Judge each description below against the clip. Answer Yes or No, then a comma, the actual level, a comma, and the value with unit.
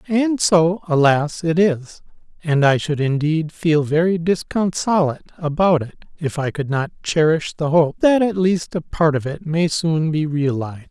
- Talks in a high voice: No, medium, 160 Hz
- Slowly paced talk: No, average, 175 wpm